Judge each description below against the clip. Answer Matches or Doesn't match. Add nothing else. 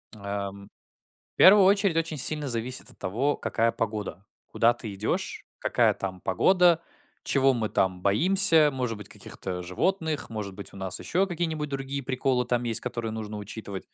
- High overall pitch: Doesn't match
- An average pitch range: Doesn't match